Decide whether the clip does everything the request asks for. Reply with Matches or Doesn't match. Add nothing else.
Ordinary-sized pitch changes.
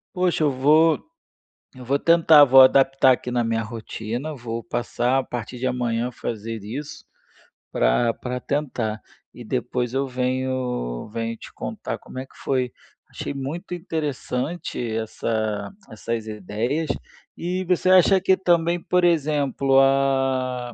Matches